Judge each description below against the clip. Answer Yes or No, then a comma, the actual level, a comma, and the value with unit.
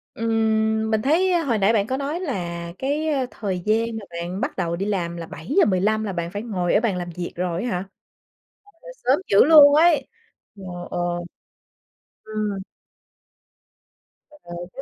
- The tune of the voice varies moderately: No, wide, 6.9 semitones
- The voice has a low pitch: No, high, 215 Hz